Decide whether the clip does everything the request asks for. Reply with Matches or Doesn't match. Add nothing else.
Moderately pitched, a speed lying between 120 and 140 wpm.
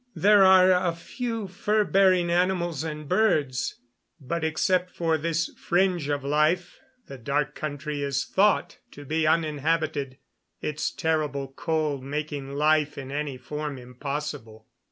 Matches